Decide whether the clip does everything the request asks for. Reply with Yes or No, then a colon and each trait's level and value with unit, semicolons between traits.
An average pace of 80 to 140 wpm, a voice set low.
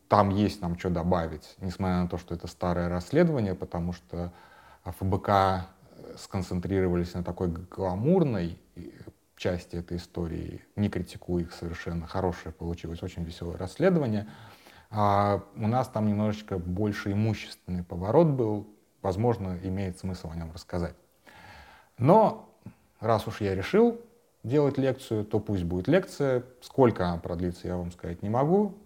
Yes: average, 135 wpm; very low, 95 Hz